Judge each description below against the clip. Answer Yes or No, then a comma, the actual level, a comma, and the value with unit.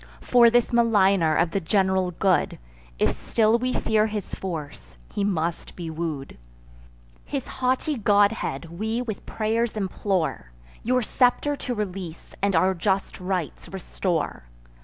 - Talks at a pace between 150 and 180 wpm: No, slow, 135 wpm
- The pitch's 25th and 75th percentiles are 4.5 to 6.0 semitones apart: Yes, average, 4.8 semitones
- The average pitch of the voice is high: Yes, high, 195 Hz